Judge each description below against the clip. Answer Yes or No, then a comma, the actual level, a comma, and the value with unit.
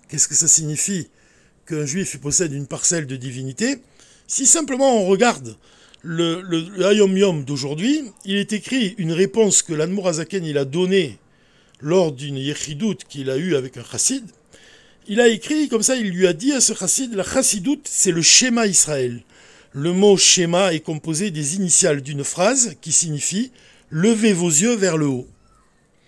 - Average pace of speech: Yes, average, 175 wpm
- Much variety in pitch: Yes, wide, 6.3 semitones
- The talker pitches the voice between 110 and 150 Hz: No, medium, 180 Hz